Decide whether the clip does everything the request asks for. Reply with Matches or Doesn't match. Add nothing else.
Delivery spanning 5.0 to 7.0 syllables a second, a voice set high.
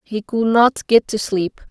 Doesn't match